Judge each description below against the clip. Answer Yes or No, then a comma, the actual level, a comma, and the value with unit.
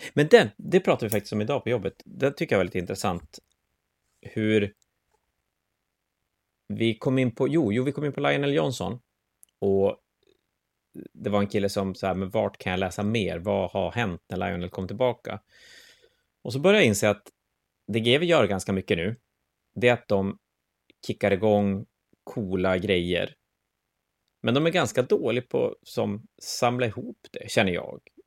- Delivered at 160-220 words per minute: Yes, average, 175 wpm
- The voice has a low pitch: Yes, low, 105 Hz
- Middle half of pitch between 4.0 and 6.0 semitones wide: Yes, average, 5.3 semitones